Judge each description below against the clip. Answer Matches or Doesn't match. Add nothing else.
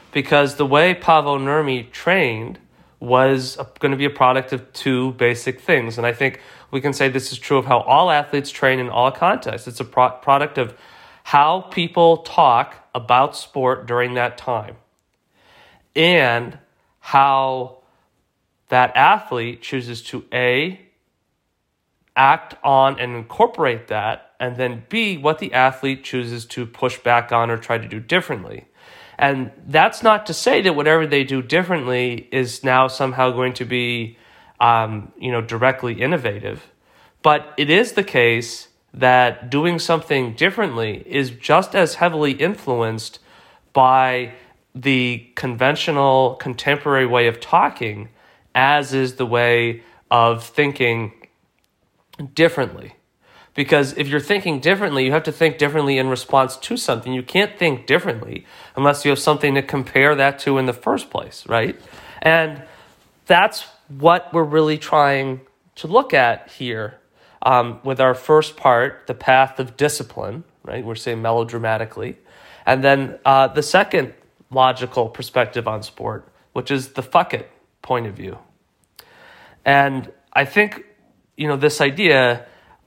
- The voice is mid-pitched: Doesn't match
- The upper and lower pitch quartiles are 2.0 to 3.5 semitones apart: Matches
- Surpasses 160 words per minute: Doesn't match